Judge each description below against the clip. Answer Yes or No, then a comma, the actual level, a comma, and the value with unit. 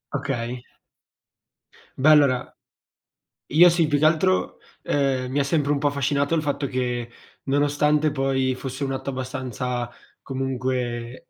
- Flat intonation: Yes, narrow, 2.3 semitones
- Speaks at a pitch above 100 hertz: Yes, low, 135 Hz